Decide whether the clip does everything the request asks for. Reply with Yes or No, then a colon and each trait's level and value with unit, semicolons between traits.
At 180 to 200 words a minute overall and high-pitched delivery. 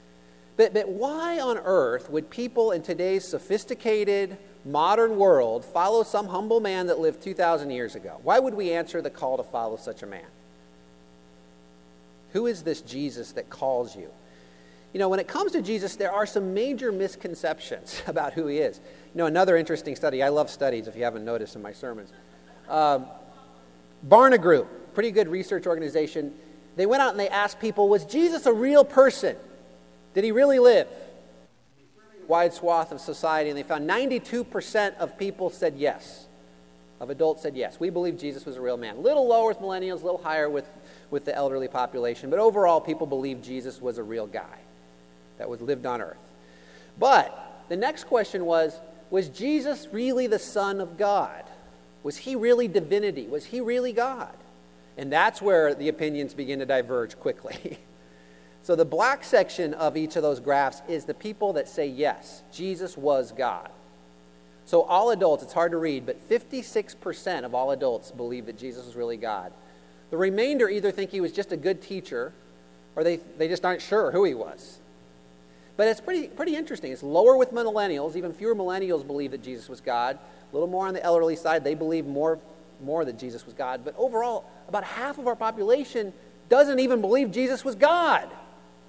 No: average, 185 wpm; medium, 165 Hz